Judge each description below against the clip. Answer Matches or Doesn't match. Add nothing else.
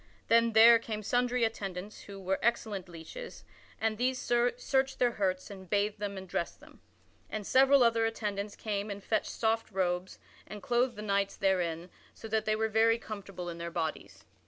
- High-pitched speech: Matches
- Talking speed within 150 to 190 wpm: Matches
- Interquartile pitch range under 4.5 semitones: Matches